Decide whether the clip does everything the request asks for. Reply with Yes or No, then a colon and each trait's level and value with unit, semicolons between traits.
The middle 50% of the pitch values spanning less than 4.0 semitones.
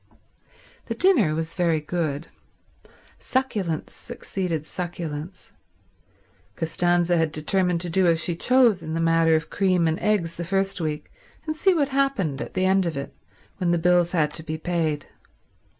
Yes: average, 2.9 semitones